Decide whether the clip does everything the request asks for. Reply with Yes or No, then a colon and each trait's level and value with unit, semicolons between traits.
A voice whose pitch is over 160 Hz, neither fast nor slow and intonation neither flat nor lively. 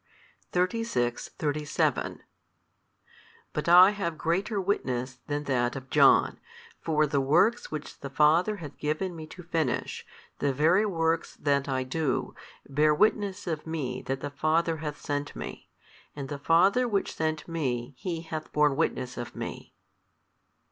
No: medium, 155 Hz; average, 145 wpm; average, 3.6 semitones